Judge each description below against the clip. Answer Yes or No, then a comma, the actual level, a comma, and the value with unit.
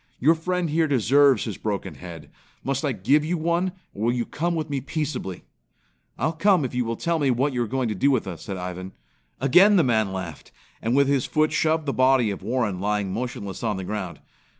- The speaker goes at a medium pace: No, fast, 220 wpm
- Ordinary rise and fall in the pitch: No, wide, 6.7 semitones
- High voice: No, low, 130 Hz